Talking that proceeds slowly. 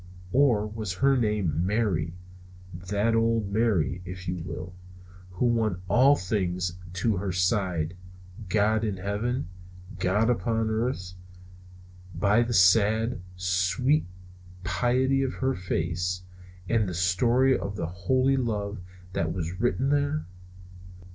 Yes: slow, 120 wpm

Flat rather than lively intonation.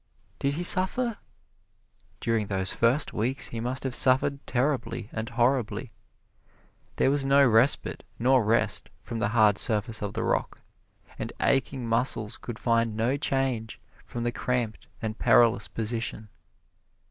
No: average, 3.1 semitones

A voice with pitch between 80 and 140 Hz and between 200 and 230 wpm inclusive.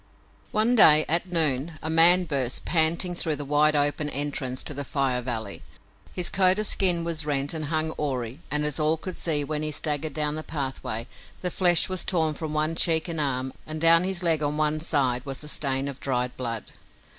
No: medium, 150 Hz; fast, 205 wpm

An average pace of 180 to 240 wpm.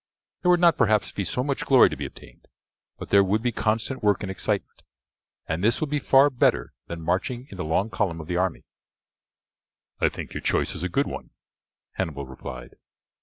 Yes: average, 200 wpm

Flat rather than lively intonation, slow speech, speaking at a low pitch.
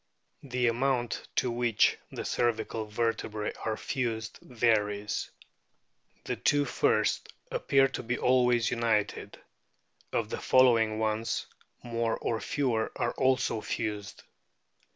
Yes: narrow, 2.2 semitones; slow, 110 wpm; low, 115 Hz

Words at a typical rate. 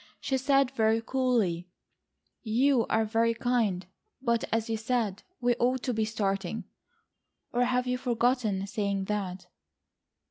No: slow, 130 wpm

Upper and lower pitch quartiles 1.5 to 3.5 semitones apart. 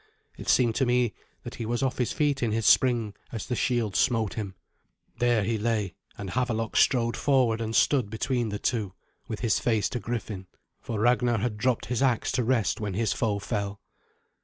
Yes: narrow, 2.6 semitones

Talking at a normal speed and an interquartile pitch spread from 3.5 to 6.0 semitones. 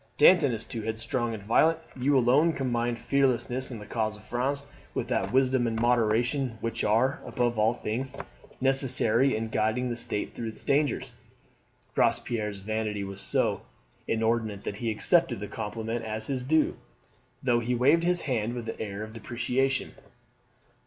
No: average, 160 wpm; average, 3.1 semitones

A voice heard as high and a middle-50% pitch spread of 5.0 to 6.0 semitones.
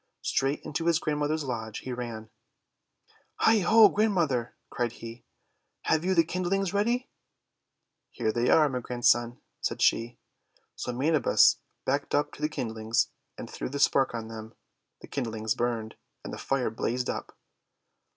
No: low, 130 Hz; wide, 5.6 semitones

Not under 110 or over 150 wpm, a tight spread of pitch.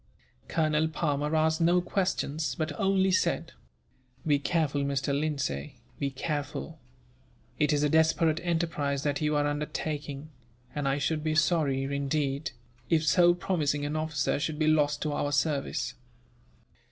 Yes: average, 140 wpm; narrow, 1.8 semitones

